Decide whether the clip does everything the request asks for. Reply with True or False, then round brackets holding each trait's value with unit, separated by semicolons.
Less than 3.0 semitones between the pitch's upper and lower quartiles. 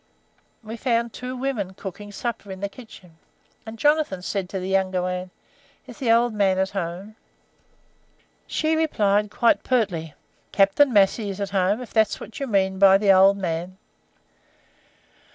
False (3.4 semitones)